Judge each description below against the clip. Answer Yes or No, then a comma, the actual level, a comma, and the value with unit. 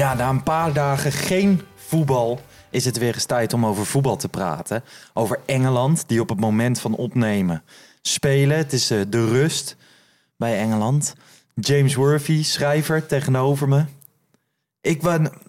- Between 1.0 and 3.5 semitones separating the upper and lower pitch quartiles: No, average, 4.1 semitones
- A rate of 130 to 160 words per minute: Yes, average, 150 wpm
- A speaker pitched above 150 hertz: No, medium, 140 Hz